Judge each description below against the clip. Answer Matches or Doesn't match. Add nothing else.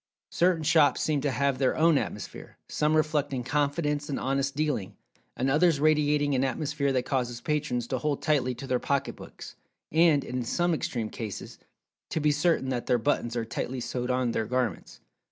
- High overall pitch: Doesn't match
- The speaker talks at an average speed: Matches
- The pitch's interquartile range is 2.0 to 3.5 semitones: Matches